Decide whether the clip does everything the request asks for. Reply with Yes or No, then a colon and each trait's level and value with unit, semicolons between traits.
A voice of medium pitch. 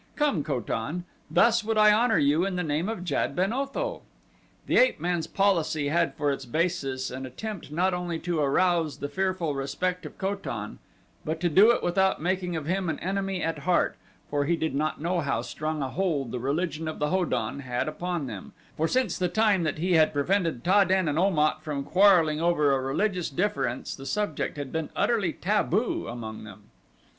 Yes: medium, 170 Hz